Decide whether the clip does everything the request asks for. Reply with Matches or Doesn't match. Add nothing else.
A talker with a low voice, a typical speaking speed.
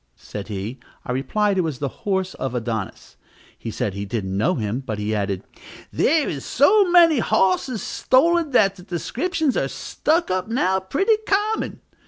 Doesn't match